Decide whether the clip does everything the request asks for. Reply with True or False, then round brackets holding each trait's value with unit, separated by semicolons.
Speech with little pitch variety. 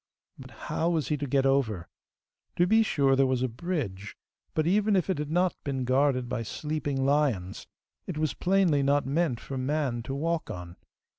False (4.0 semitones)